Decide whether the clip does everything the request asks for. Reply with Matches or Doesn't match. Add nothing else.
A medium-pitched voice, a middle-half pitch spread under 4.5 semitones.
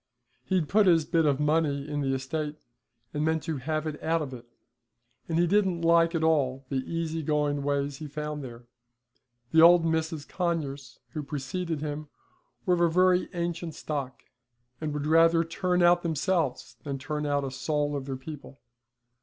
Matches